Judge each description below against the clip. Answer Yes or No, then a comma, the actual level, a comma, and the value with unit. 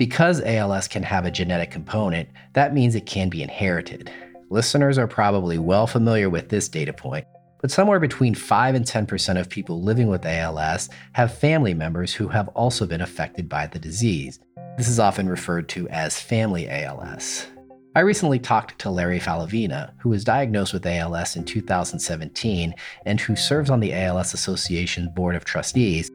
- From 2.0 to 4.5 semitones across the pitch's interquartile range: No, wide, 5.6 semitones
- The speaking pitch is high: No, low, 100 Hz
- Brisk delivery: No, average, 170 wpm